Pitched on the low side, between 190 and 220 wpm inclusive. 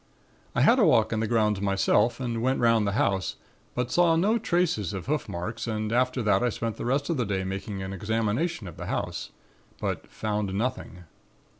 Yes: low, 110 Hz; average, 200 wpm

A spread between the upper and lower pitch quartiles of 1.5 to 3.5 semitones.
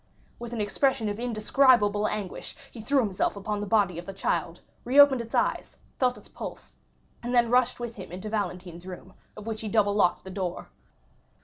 No: average, 3.9 semitones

